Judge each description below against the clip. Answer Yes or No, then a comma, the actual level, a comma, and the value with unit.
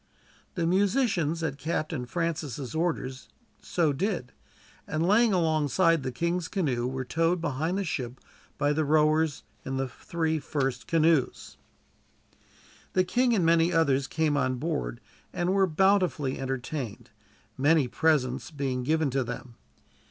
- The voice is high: No, medium, 155 Hz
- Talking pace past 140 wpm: No, slow, 135 wpm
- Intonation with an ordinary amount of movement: Yes, average, 4.2 semitones